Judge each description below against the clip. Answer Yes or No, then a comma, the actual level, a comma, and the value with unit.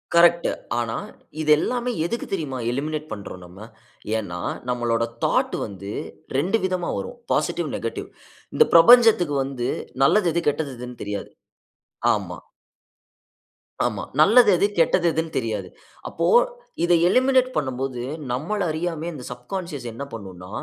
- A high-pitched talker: No, medium, 150 Hz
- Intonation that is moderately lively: No, wide, 6.6 semitones